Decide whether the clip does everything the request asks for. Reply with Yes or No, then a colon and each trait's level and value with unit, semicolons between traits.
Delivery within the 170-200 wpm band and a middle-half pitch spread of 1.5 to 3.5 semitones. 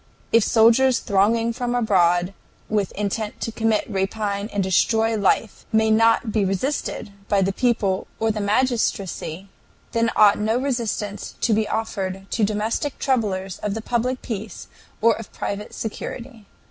No: average, 145 wpm; narrow, 2.4 semitones